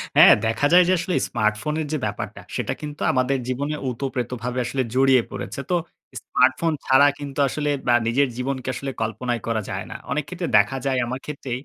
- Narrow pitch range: No, average, 3.0 semitones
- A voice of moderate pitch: No, low, 130 Hz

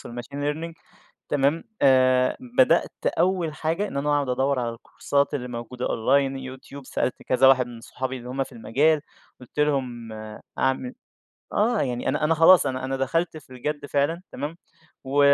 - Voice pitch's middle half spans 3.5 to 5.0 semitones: No, average, 2.8 semitones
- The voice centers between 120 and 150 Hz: Yes, low, 135 Hz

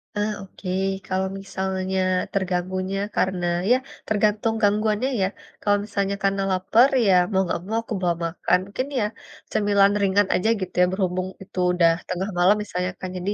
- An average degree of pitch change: No, narrow, 1.9 semitones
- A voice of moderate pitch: No, high, 195 Hz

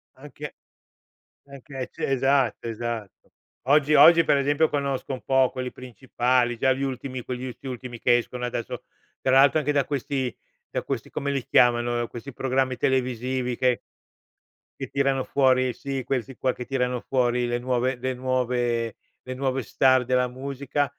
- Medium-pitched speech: No, low, 130 Hz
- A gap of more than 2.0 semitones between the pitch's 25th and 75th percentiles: No, narrow, 1.7 semitones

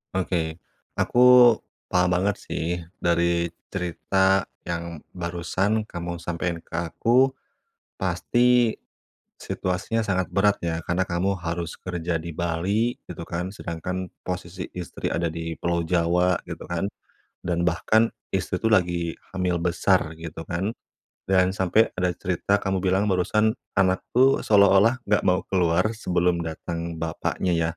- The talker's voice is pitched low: Yes, very low, 90 Hz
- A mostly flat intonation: Yes, narrow, 2.2 semitones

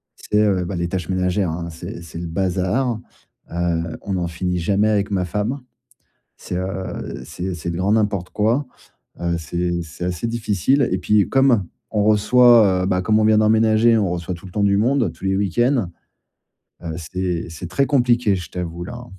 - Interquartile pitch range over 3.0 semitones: Yes, average, 3.7 semitones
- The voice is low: Yes, very low, 95 Hz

